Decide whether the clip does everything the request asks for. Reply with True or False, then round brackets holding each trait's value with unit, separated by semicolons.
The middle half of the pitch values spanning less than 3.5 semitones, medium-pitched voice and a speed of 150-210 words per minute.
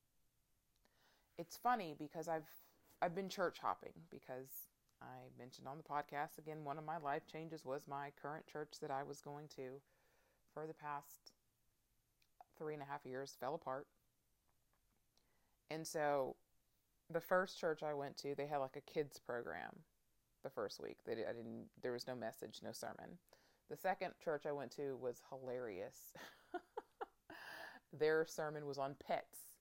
True (3.1 semitones; 145 Hz; 160 wpm)